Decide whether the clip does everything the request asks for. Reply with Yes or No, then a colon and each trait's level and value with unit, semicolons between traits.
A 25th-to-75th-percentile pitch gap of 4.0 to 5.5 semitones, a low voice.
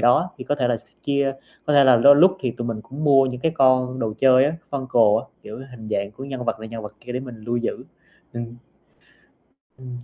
No: average, 2.7 semitones; low, 125 Hz